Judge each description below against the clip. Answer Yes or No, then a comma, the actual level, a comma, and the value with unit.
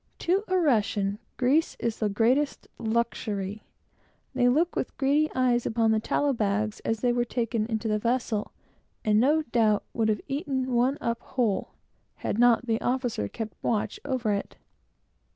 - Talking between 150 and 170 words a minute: Yes, average, 160 wpm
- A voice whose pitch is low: No, high, 235 Hz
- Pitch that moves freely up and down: No, average, 3.2 semitones